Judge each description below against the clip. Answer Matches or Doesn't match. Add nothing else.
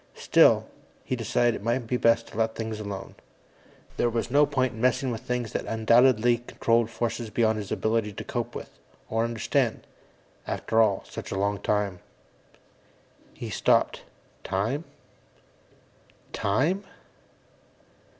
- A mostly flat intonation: Matches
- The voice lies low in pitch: Matches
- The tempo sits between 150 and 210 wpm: Doesn't match